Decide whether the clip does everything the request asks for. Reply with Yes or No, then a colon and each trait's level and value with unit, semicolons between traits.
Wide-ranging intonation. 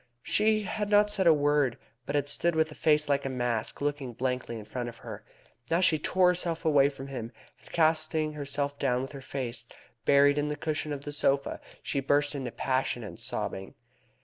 No: average, 3.3 semitones